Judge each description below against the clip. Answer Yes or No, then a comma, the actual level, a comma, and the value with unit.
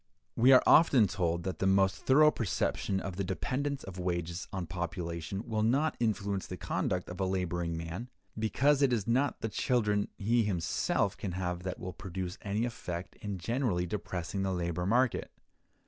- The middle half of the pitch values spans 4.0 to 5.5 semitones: Yes, average, 4.6 semitones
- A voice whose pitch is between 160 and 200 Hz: No, very low, 95 Hz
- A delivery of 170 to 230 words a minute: Yes, average, 175 wpm